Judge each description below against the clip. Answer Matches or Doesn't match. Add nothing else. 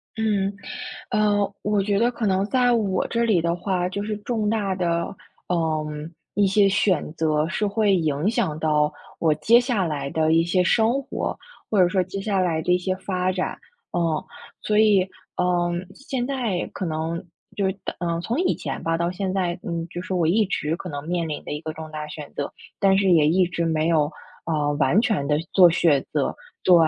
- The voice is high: Doesn't match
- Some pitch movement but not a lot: Matches